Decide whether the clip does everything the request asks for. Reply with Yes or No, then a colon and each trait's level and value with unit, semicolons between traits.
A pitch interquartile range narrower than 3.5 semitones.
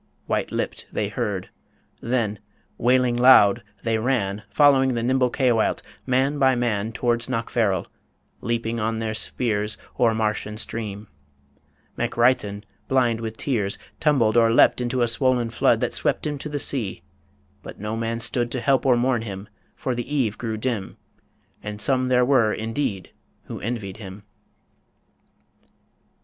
Yes: average, 2.9 semitones